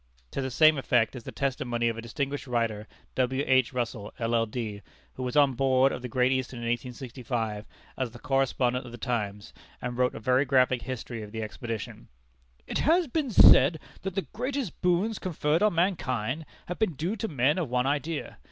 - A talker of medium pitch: No, low, 130 Hz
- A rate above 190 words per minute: Yes, average, 200 wpm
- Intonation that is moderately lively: Yes, average, 4.1 semitones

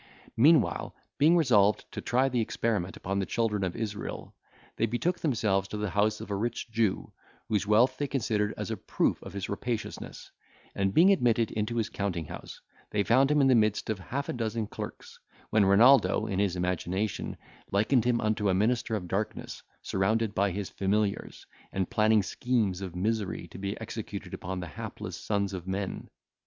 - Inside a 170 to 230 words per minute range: Yes, average, 180 wpm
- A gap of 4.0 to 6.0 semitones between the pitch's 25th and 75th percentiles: No, average, 3.2 semitones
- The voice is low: Yes, low, 105 Hz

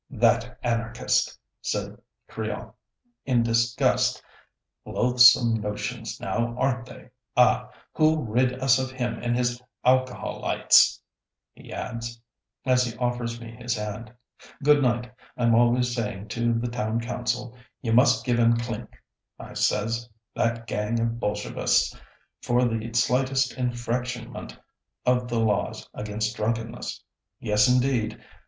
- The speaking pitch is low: Yes, low, 120 Hz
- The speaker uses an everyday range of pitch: No, narrow, 1.4 semitones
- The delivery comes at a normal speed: No, slow, 125 wpm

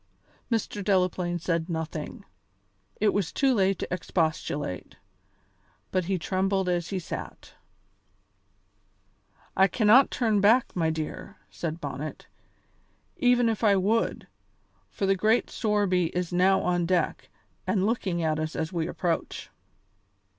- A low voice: No, medium, 185 Hz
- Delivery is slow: Yes, slow, 125 wpm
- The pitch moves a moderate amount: Yes, average, 3.6 semitones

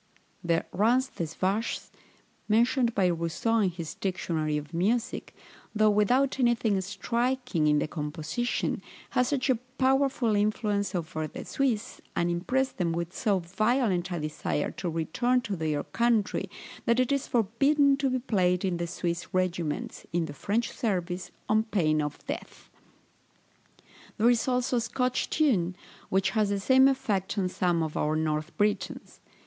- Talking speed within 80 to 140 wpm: No, average, 155 wpm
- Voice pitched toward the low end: No, high, 200 Hz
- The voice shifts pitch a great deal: Yes, wide, 6.0 semitones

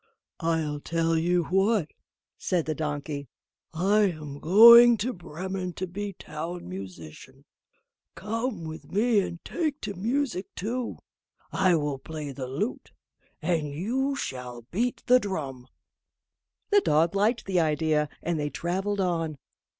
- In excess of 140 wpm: No, slow, 135 wpm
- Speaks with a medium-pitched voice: Yes, medium, 175 Hz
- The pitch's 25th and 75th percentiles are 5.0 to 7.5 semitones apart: Yes, average, 5.3 semitones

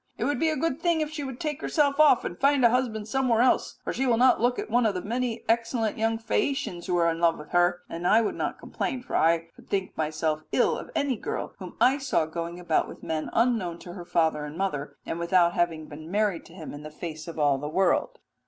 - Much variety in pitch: Yes, wide, 7.0 semitones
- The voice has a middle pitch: No, high, 195 Hz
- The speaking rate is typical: No, fast, 255 wpm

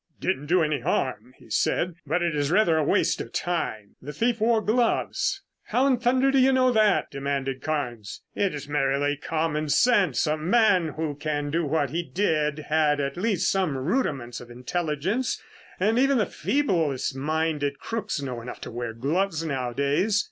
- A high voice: No, medium, 155 Hz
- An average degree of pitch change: No, wide, 6.3 semitones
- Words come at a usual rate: Yes, average, 175 wpm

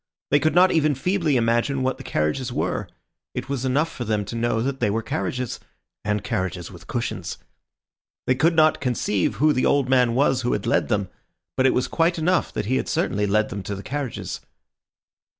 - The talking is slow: No, fast, 205 wpm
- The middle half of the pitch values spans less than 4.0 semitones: No, average, 5.0 semitones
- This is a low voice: Yes, low, 125 Hz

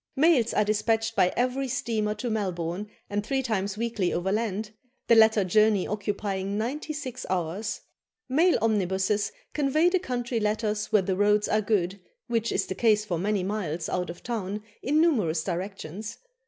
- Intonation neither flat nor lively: Yes, average, 3.3 semitones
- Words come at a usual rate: Yes, average, 160 wpm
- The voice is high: Yes, high, 210 Hz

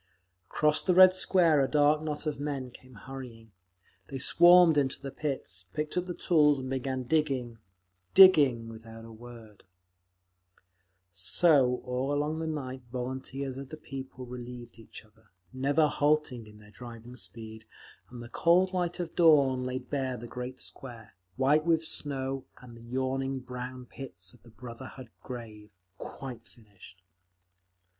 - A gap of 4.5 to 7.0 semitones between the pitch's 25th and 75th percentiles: No, average, 3.7 semitones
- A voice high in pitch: No, low, 130 Hz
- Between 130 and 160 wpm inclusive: Yes, average, 150 wpm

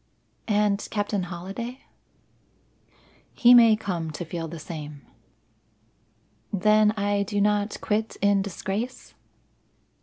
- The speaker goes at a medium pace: No, slow, 100 wpm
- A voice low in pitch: No, high, 205 Hz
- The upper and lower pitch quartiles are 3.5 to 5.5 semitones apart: No, average, 3.1 semitones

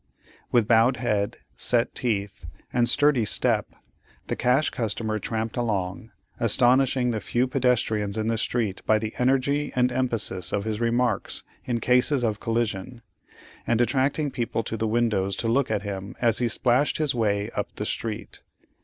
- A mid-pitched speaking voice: No, low, 115 Hz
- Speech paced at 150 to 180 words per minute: Yes, average, 160 wpm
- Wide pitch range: No, narrow, 2.6 semitones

